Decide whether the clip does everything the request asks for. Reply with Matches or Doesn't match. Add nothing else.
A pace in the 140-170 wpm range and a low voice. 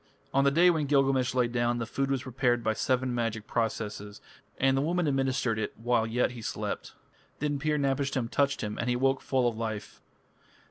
Doesn't match